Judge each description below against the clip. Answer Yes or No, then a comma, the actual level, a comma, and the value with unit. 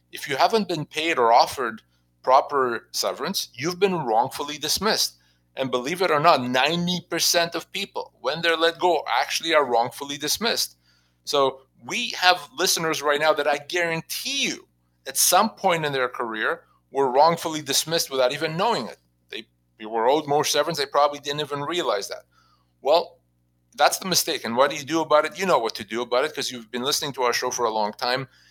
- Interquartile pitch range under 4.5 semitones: No, wide, 5.5 semitones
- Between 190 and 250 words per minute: Yes, average, 195 wpm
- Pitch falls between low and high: Yes, medium, 145 Hz